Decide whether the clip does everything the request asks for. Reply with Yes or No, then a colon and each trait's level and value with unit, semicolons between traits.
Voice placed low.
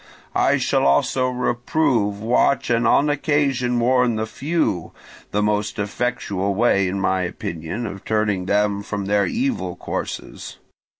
Yes: low, 110 Hz